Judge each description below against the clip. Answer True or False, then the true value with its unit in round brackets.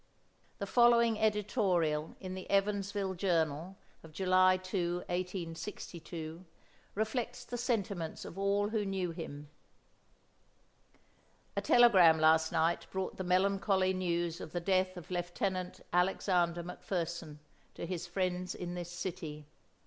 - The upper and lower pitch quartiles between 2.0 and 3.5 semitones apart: True (2.4 semitones)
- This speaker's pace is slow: True (120 wpm)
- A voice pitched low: False (185 Hz)